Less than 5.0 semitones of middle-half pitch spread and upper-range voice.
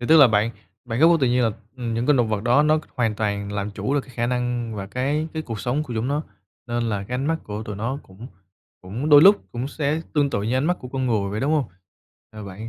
No: average, 4.6 semitones; low, 120 Hz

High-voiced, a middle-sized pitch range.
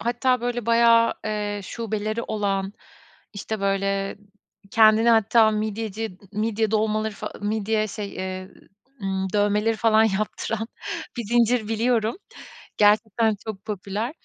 No: high, 215 Hz; narrow, 1.8 semitones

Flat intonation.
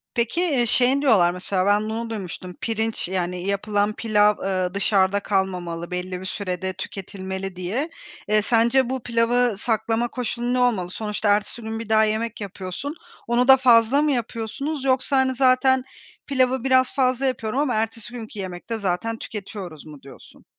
No: average, 4.5 semitones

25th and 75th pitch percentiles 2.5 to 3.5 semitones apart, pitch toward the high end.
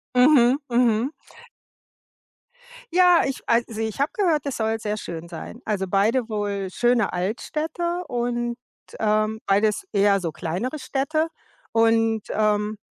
No: average, 3.9 semitones; high, 225 Hz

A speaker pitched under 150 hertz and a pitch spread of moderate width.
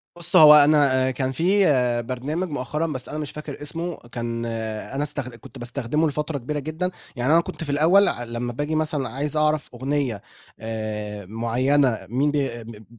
Yes: medium, 140 Hz; average, 4.3 semitones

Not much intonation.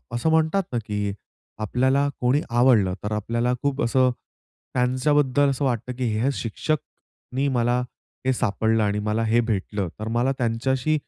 No: average, 3.2 semitones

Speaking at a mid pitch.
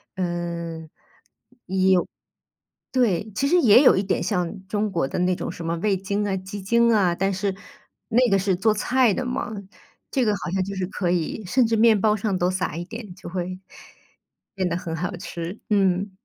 No: high, 195 Hz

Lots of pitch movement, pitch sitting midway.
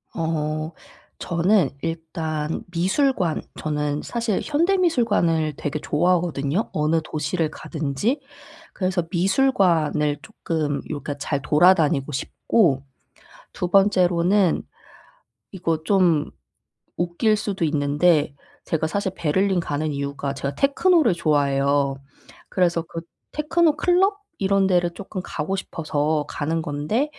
No: average, 4.5 semitones; medium, 165 Hz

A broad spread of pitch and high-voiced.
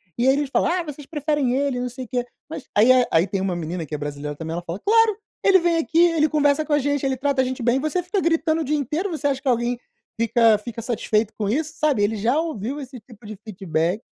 Yes: wide, 6.0 semitones; very high, 260 Hz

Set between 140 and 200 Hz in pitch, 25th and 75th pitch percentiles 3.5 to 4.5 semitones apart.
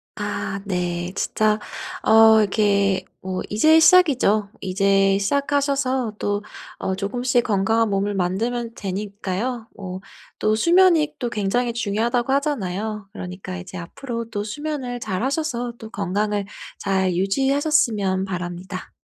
No: high, 210 Hz; average, 4.1 semitones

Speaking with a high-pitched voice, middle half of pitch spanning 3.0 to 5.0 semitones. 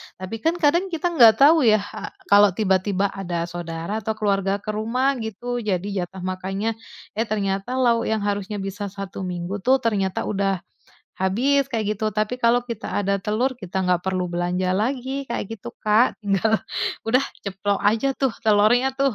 Yes: high, 210 Hz; average, 3.6 semitones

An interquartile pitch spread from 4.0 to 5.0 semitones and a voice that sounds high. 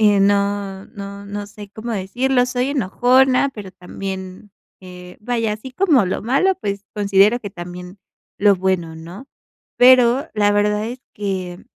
Yes: average, 4.3 semitones; high, 205 Hz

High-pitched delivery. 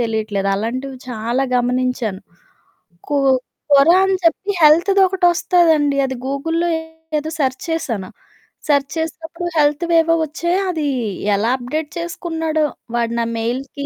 Yes: very high, 290 Hz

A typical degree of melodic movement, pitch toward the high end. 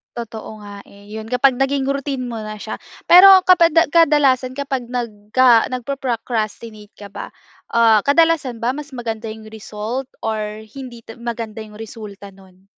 Yes: average, 3.9 semitones; high, 235 Hz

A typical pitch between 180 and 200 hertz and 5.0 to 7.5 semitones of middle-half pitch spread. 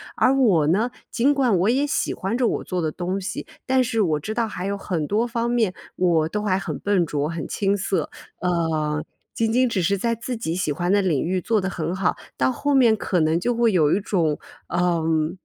Yes: high, 190 Hz; wide, 5.4 semitones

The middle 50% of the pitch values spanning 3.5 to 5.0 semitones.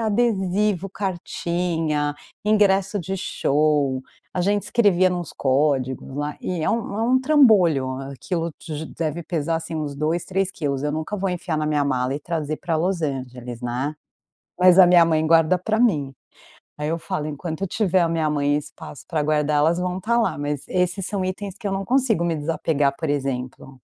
Yes: average, 4.5 semitones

